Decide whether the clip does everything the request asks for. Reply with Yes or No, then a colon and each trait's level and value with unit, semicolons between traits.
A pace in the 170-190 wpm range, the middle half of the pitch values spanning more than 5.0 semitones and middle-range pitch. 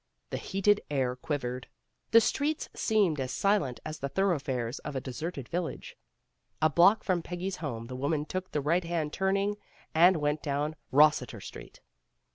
No: average, 160 wpm; wide, 5.4 semitones; medium, 155 Hz